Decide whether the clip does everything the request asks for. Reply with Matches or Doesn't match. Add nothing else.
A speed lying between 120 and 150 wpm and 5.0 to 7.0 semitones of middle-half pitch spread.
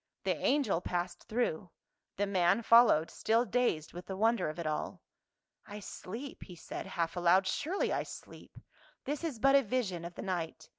Doesn't match